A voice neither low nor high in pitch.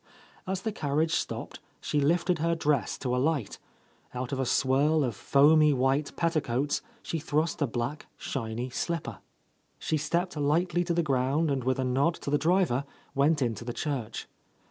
Yes: medium, 145 Hz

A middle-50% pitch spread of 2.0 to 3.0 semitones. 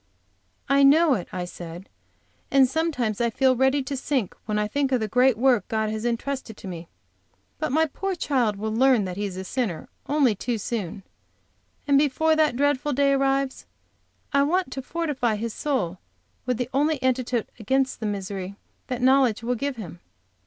No: average, 4.5 semitones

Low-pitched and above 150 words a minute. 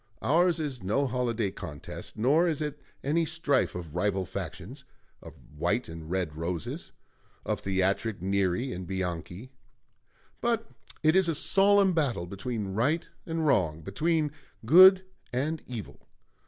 No: low, 125 Hz; slow, 135 wpm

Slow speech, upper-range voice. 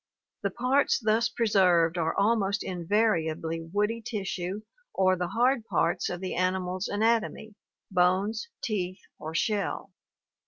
Yes: slow, 125 wpm; high, 195 Hz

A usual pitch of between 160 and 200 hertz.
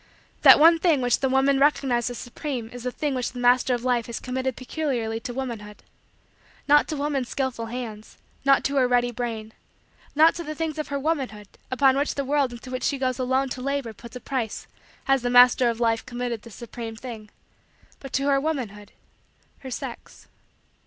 No: very high, 255 Hz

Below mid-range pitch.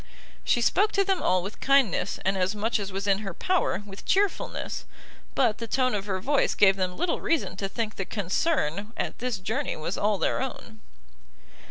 No: high, 210 Hz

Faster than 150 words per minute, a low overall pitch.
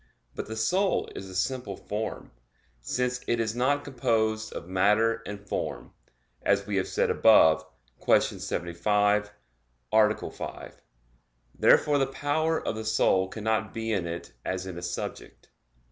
No: average, 145 wpm; low, 110 Hz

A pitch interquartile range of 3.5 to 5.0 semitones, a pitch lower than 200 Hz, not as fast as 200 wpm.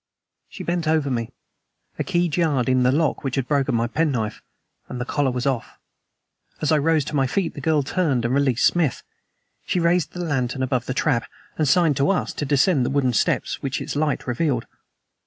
No: average, 3.8 semitones; medium, 140 Hz; fast, 205 wpm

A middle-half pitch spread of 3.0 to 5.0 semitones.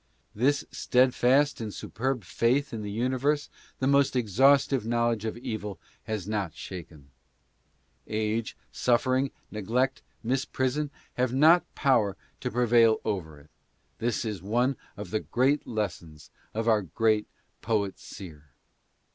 Yes: average, 3.9 semitones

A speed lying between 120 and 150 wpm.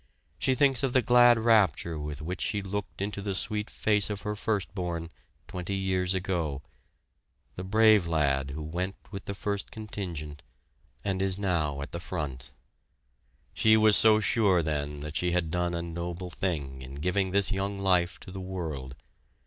No: average, 175 wpm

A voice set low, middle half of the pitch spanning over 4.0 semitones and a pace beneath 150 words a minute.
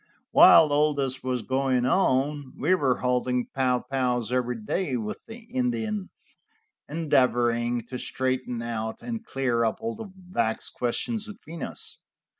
Yes: low, 130 Hz; wide, 5.4 semitones; average, 140 wpm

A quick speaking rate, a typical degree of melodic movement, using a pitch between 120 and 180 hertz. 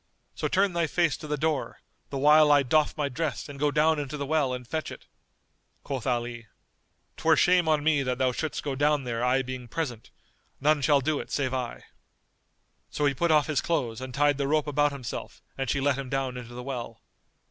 Yes: fast, 215 wpm; average, 3.0 semitones; medium, 140 Hz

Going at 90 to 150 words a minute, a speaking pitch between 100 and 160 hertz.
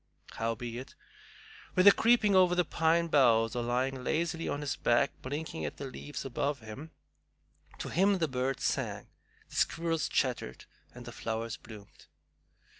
Yes: average, 145 wpm; low, 135 Hz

